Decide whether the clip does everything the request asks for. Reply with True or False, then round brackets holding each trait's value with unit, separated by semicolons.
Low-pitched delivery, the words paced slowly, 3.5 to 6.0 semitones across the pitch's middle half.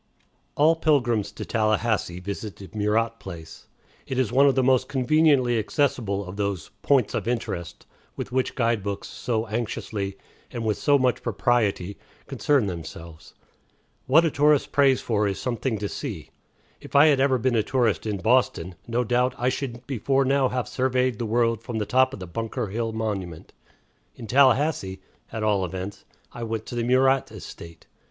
False (115 Hz; 175 wpm; 4.1 semitones)